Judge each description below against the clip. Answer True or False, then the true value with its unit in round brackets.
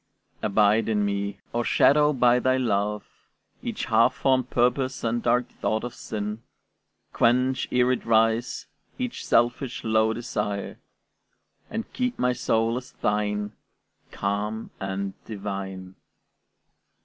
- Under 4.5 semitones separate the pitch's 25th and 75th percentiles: True (3.3 semitones)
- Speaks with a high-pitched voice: False (115 Hz)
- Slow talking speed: True (115 wpm)